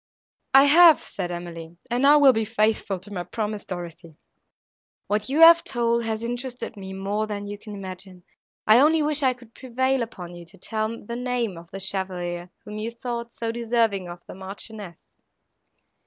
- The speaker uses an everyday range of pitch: Yes, average, 4.2 semitones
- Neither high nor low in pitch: No, high, 215 Hz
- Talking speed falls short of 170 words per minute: No, average, 175 wpm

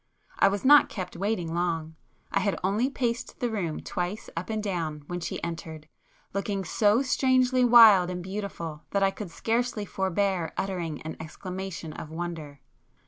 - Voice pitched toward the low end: No, high, 190 Hz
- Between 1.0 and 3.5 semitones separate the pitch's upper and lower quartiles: No, average, 4.3 semitones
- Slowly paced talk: No, average, 160 wpm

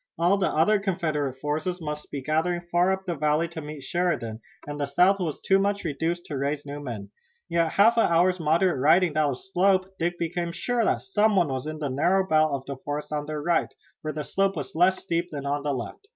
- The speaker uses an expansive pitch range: No, average, 3.8 semitones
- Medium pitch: Yes, medium, 160 Hz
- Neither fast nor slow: No, fast, 230 wpm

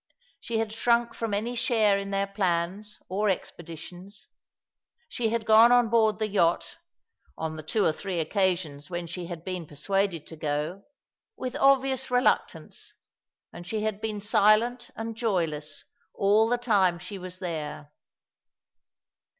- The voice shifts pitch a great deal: No, average, 4.4 semitones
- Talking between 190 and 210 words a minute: No, average, 150 wpm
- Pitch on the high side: Yes, high, 200 Hz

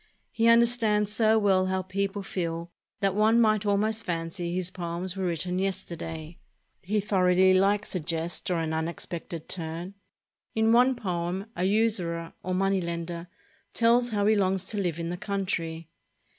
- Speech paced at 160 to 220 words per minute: Yes, average, 170 wpm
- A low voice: No, medium, 185 Hz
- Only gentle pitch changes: No, average, 3.4 semitones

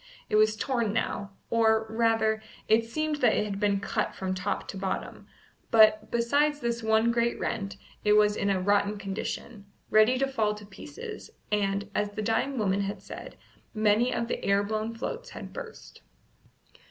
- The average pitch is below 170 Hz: No, high, 215 Hz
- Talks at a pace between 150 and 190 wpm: Yes, average, 175 wpm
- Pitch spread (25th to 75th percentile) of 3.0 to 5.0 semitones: No, narrow, 2.4 semitones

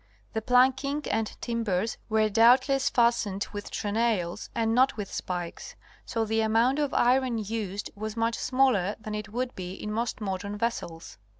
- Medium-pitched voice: No, high, 225 Hz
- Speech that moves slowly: No, average, 160 wpm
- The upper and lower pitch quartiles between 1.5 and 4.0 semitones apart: Yes, average, 2.9 semitones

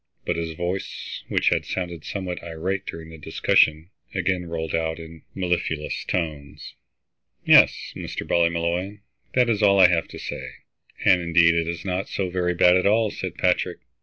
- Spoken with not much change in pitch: Yes, narrow, 2.2 semitones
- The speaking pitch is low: Yes, very low, 85 Hz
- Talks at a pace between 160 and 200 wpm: Yes, average, 165 wpm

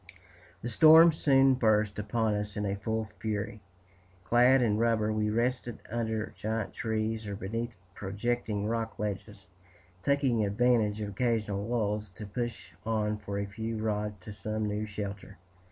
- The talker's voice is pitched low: Yes, low, 110 Hz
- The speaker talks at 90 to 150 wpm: Yes, average, 145 wpm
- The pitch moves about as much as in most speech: No, narrow, 2.0 semitones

